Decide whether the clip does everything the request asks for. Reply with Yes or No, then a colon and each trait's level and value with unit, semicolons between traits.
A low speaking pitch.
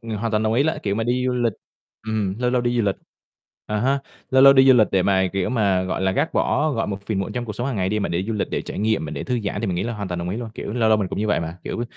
Yes: low, 110 Hz